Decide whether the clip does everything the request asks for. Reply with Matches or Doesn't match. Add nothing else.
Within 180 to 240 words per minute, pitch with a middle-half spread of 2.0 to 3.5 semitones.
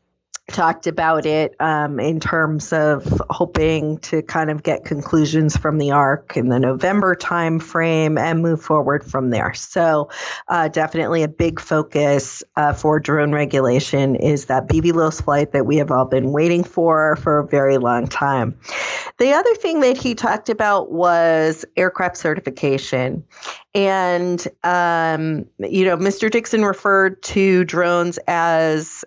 Doesn't match